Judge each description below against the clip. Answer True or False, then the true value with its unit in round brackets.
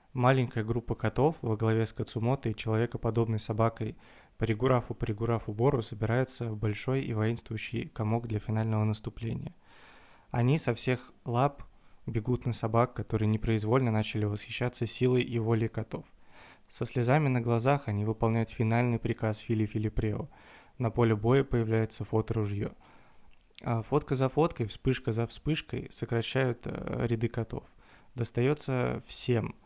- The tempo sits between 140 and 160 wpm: False (125 wpm)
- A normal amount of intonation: False (2.0 semitones)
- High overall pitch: False (115 Hz)